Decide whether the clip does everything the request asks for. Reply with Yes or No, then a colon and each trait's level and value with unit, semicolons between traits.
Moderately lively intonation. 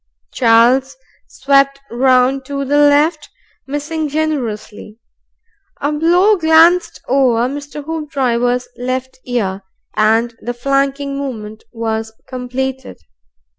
Yes: average, 3.2 semitones